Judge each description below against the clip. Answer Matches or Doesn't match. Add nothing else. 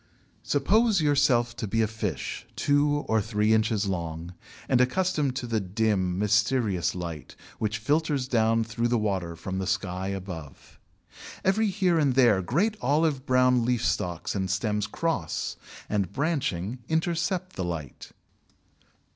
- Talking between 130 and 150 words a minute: Matches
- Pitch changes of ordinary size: Doesn't match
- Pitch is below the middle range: Matches